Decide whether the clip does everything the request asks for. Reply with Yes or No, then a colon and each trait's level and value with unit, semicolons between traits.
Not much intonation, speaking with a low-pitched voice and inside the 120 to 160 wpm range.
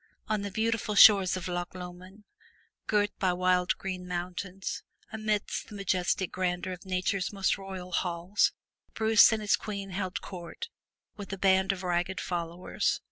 No: narrow, 2.0 semitones; high, 190 Hz; average, 150 wpm